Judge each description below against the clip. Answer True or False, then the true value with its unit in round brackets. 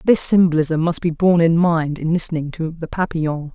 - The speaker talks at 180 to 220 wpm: True (205 wpm)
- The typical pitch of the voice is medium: True (165 Hz)